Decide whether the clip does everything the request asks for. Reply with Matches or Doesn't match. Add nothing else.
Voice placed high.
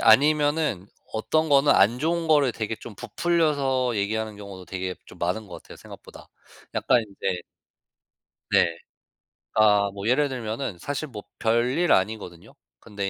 Doesn't match